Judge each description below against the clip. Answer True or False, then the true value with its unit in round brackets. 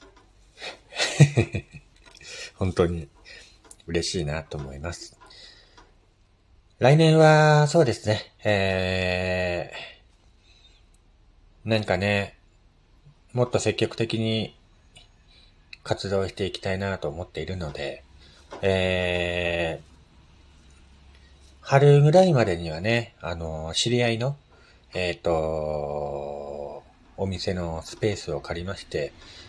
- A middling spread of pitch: True (4.8 semitones)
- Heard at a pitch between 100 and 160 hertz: False (90 Hz)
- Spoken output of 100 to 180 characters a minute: True (175 characters per minute)